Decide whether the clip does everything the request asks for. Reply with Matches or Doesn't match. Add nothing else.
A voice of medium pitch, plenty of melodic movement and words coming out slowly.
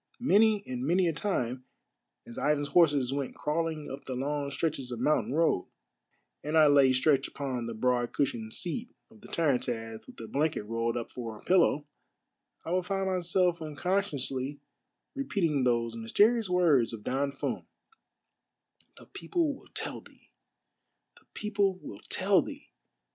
Doesn't match